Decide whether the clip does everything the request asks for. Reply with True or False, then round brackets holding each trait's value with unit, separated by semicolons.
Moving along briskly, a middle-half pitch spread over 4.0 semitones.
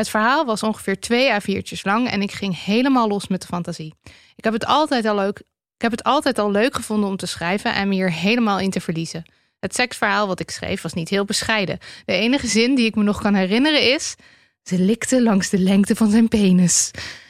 False (230 wpm; 3.3 semitones)